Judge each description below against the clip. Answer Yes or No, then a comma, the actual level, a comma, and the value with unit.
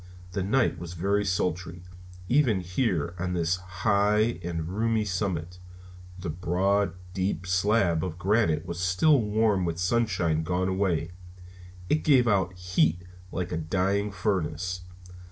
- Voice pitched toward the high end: No, very low, 90 Hz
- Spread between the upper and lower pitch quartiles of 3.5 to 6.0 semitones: No, average, 2.8 semitones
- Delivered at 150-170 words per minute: No, slow, 135 wpm